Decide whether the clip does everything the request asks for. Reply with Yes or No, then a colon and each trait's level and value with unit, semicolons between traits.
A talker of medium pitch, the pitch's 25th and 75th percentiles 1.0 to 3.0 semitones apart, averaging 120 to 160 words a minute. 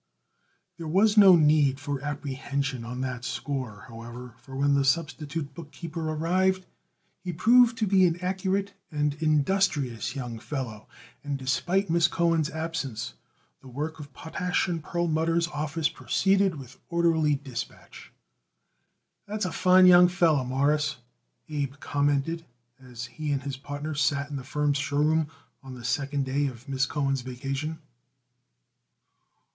No: medium, 150 Hz; average, 3.7 semitones; average, 140 wpm